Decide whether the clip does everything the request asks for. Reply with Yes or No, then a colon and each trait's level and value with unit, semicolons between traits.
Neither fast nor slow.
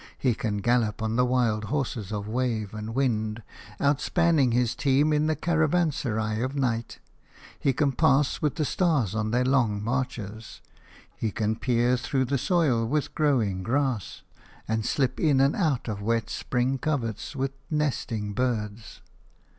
Yes: average, 155 wpm